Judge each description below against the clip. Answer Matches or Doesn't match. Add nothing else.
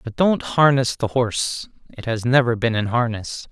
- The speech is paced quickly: Doesn't match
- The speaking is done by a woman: Doesn't match